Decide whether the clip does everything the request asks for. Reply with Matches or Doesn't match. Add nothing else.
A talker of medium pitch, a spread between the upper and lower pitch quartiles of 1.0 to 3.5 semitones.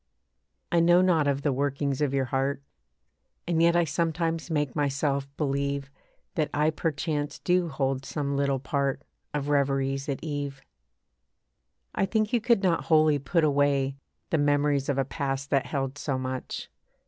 Matches